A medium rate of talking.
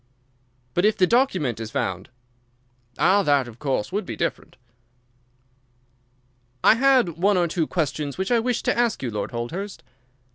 Yes: average, 155 wpm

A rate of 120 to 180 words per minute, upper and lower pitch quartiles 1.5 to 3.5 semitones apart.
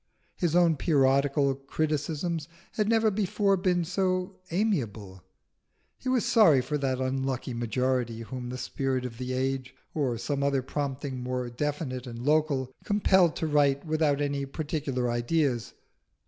No: average, 140 wpm; average, 4.2 semitones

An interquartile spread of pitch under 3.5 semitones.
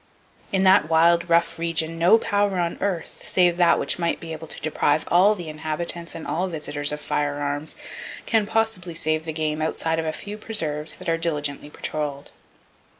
Yes: narrow, 2.5 semitones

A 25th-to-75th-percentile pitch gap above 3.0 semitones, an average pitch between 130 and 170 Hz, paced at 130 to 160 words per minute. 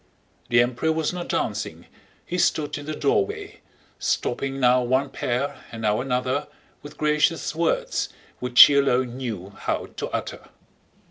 Yes: average, 4.1 semitones; low, 135 Hz; average, 145 wpm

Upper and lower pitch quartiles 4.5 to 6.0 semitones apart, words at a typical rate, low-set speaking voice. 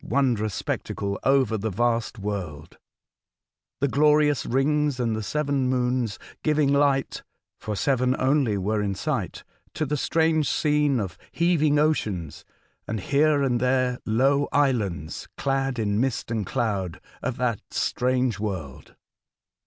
No: average, 4.9 semitones; slow, 130 wpm; low, 125 Hz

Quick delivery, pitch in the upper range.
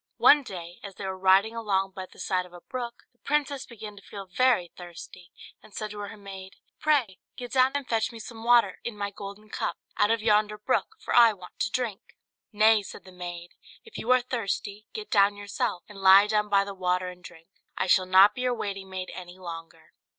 Yes: fast, 220 wpm; high, 205 Hz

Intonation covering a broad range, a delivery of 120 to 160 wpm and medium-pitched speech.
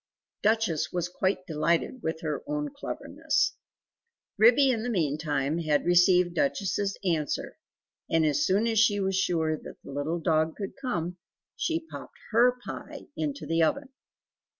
Yes: wide, 6.1 semitones; average, 150 wpm; medium, 180 Hz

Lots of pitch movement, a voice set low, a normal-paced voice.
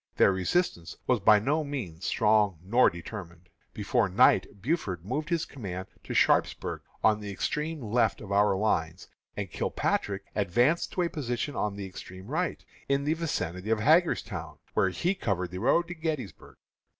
Yes: wide, 7.7 semitones; low, 110 Hz; average, 160 wpm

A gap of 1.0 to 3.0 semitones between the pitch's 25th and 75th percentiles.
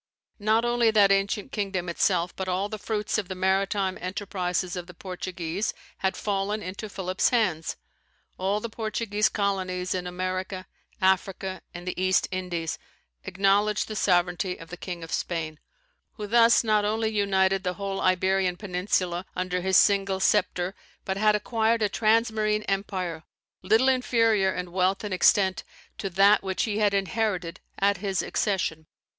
Yes: narrow, 2.4 semitones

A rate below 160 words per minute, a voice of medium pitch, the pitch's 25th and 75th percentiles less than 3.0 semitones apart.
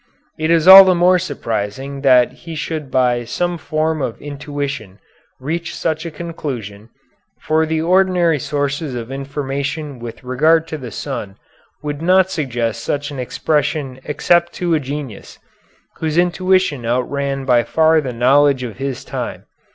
No: average, 150 wpm; medium, 145 Hz; average, 4.0 semitones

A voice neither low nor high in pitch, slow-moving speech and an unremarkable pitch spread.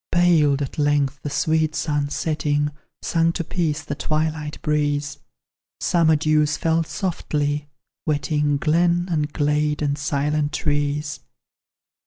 No: medium, 150 Hz; slow, 120 wpm; narrow, 1.4 semitones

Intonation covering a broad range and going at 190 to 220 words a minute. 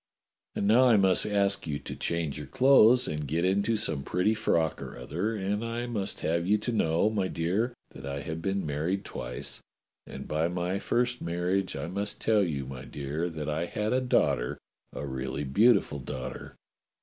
Yes: wide, 5.9 semitones; average, 195 wpm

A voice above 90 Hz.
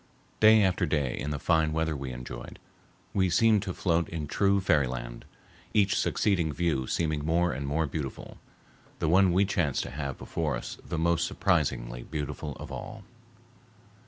No: very low, 80 Hz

